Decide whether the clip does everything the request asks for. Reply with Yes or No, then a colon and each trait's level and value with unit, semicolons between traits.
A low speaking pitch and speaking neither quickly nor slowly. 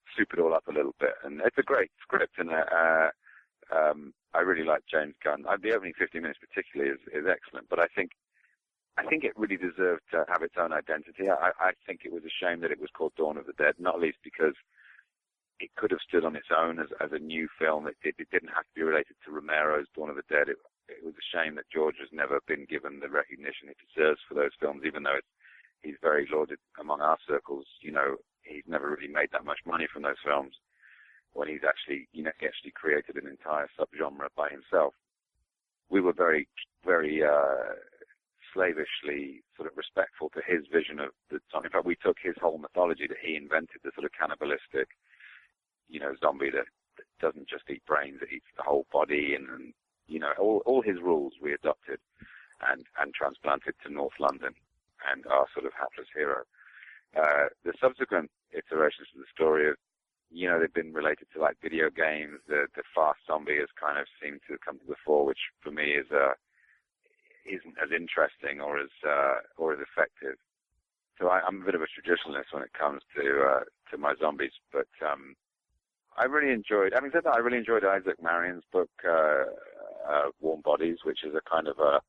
No: very low, 85 Hz; fast, 210 wpm